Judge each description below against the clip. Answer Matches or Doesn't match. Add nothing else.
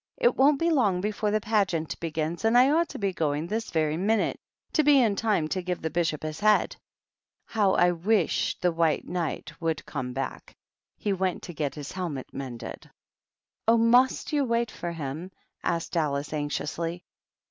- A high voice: Doesn't match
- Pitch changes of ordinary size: Doesn't match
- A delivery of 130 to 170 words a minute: Doesn't match